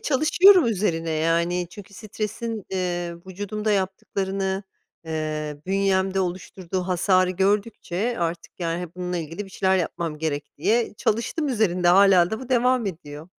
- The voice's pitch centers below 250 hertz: Yes, high, 190 Hz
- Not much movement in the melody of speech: No, average, 3.3 semitones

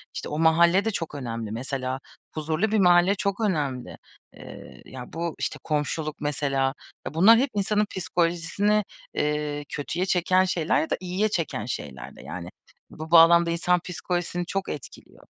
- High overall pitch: No, medium, 165 Hz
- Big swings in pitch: No, average, 3.9 semitones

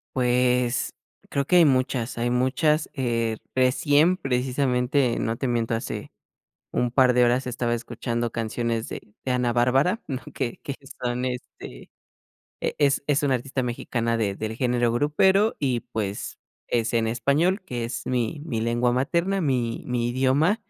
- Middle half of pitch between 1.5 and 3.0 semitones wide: Yes, average, 2.7 semitones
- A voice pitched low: Yes, low, 125 Hz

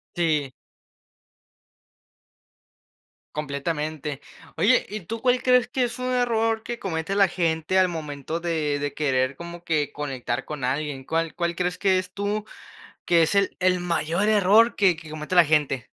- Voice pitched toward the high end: No, medium, 170 Hz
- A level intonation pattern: No, average, 4.9 semitones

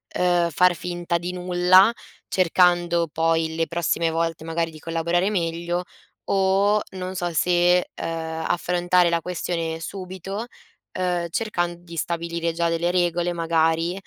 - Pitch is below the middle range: No, medium, 175 Hz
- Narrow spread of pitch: Yes, narrow, 1.4 semitones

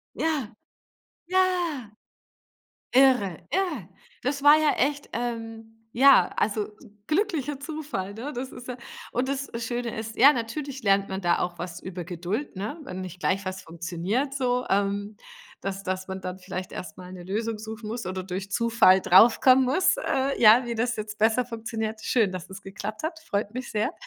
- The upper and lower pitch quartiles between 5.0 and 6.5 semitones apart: Yes, wide, 5.5 semitones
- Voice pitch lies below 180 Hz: No, high, 225 Hz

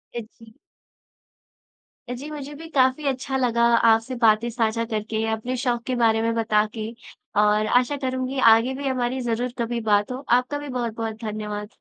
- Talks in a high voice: Yes, high, 235 Hz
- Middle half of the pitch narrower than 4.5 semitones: Yes, narrow, 2.6 semitones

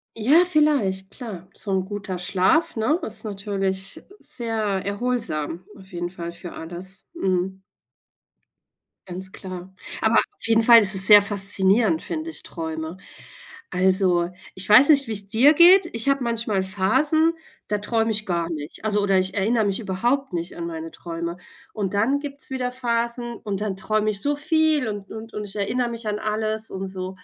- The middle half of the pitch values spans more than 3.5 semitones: Yes, average, 4.0 semitones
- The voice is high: Yes, high, 205 Hz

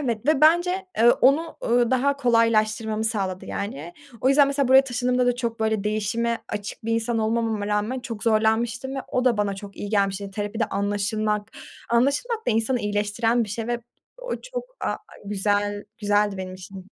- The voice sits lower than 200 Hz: No, high, 225 Hz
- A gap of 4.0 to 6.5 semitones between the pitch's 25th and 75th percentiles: No, average, 3.3 semitones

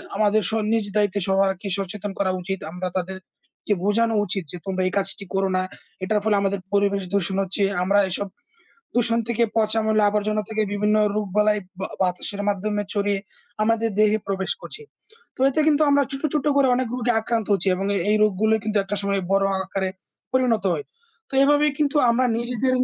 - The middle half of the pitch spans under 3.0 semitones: Yes, narrow, 2.5 semitones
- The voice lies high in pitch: Yes, high, 210 Hz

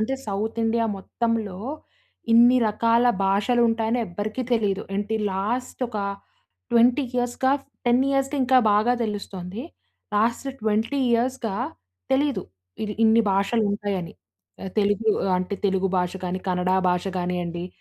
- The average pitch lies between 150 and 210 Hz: No, high, 220 Hz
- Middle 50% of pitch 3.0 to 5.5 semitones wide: Yes, average, 3.5 semitones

